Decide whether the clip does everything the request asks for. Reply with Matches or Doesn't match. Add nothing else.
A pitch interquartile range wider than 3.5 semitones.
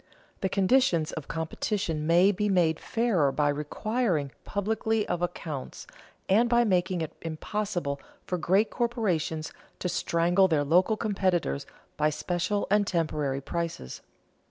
Matches